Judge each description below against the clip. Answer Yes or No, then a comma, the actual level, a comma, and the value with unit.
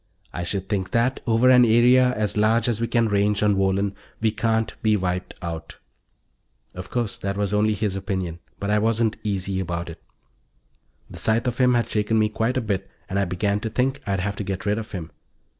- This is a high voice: No, low, 105 Hz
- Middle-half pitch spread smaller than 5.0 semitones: Yes, average, 2.8 semitones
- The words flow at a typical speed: No, fast, 210 wpm